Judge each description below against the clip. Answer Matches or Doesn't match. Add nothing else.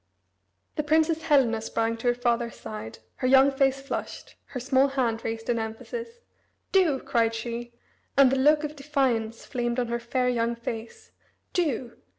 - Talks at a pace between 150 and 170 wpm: Matches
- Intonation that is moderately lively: Matches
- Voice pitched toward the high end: Matches